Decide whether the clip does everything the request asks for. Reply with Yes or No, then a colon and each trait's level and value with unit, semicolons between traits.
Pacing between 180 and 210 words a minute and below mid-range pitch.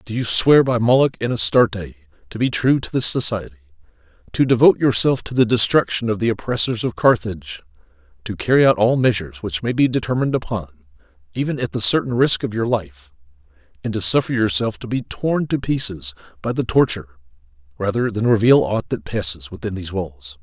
Yes: average, 185 wpm; low, 105 Hz